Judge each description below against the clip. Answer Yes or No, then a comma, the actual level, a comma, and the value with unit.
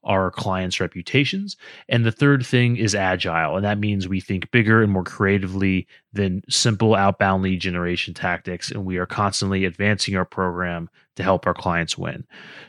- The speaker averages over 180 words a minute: No, average, 170 wpm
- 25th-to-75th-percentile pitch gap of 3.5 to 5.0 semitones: No, average, 3.0 semitones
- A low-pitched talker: Yes, very low, 95 Hz